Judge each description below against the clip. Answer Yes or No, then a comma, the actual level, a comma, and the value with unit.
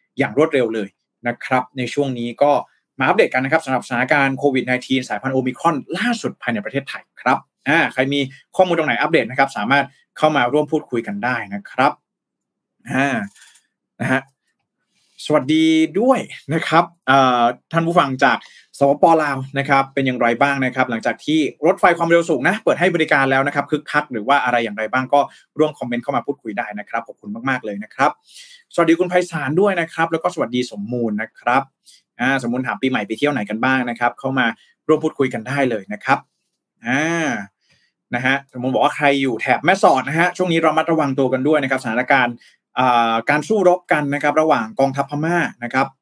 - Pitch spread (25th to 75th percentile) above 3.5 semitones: Yes, average, 4.0 semitones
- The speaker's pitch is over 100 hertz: Yes, medium, 140 Hz